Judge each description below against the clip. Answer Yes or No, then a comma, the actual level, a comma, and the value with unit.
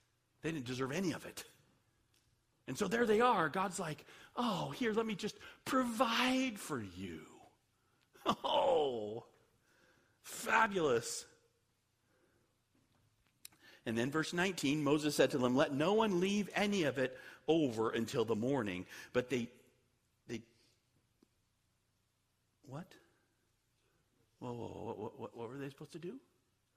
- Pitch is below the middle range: Yes, low, 130 Hz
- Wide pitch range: Yes, wide, 8.4 semitones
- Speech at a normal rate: No, slow, 125 wpm